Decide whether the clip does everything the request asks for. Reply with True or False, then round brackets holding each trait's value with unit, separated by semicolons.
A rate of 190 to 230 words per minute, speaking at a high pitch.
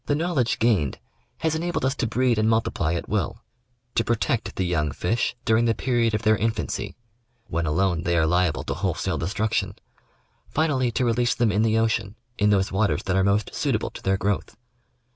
False (205 wpm; 110 Hz)